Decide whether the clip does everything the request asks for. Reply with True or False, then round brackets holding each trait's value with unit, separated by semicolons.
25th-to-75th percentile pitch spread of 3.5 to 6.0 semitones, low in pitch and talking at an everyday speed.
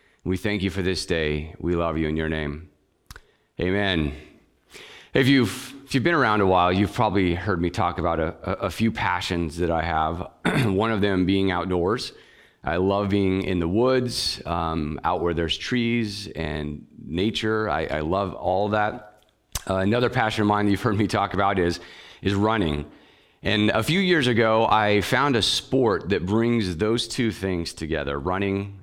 True (4.1 semitones; 100 Hz; 180 wpm)